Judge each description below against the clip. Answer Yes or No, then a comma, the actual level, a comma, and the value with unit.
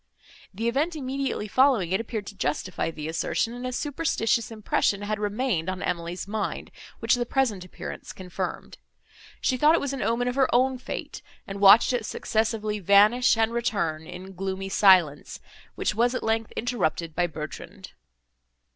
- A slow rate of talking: No, average, 165 wpm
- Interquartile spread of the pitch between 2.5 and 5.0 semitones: Yes, average, 4.7 semitones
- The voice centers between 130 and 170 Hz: No, high, 215 Hz